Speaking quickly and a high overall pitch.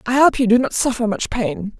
Yes: fast, 270 wpm; high, 235 Hz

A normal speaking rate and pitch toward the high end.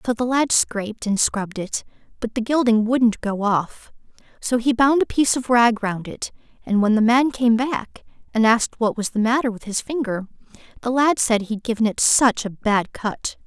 No: fast, 210 wpm; high, 230 Hz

